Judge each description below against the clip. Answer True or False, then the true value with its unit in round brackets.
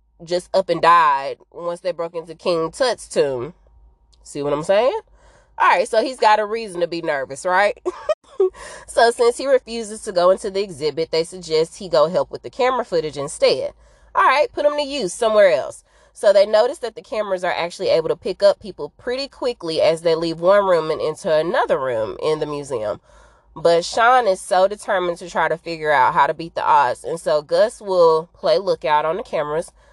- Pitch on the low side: False (200 Hz)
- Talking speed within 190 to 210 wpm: True (205 wpm)